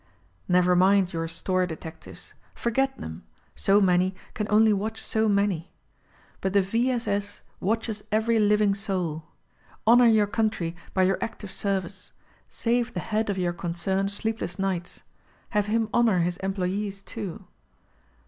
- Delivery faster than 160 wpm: No, average, 155 wpm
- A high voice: Yes, high, 200 Hz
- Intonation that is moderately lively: Yes, average, 3.2 semitones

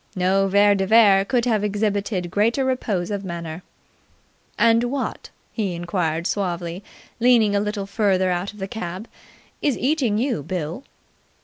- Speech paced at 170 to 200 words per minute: No, average, 145 wpm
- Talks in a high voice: Yes, high, 200 Hz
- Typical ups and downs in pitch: Yes, average, 3.7 semitones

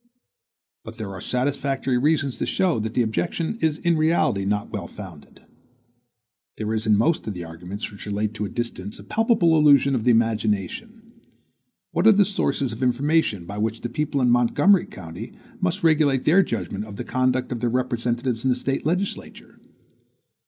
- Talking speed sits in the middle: Yes, average, 175 wpm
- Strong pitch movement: Yes, wide, 6.2 semitones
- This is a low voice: Yes, low, 125 Hz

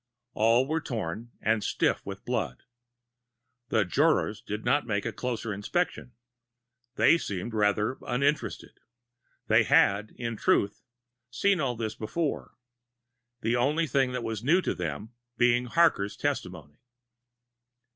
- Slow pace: Yes, slow, 125 wpm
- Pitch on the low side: Yes, low, 115 Hz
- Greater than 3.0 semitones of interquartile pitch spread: Yes, average, 4.8 semitones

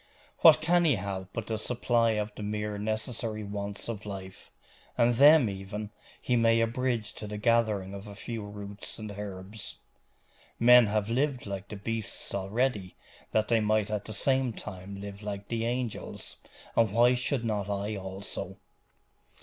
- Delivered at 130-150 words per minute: No, average, 165 wpm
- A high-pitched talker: No, low, 105 Hz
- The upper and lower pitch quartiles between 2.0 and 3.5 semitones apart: Yes, narrow, 2.6 semitones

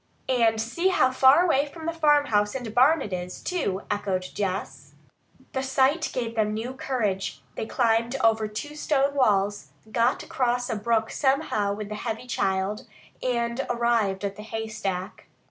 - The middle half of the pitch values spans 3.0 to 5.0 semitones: Yes, average, 4.2 semitones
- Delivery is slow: No, average, 160 wpm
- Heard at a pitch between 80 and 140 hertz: No, high, 230 Hz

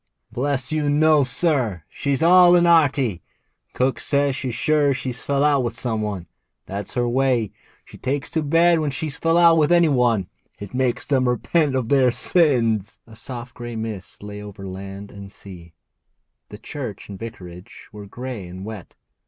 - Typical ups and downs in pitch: No, wide, 5.7 semitones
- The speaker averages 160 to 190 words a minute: Yes, average, 175 wpm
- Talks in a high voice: No, low, 125 Hz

